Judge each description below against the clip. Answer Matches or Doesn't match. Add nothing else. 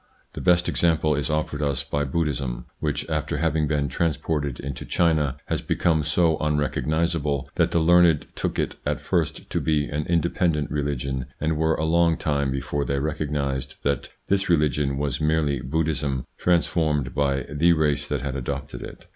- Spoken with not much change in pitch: Matches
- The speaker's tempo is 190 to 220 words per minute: Doesn't match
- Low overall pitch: Matches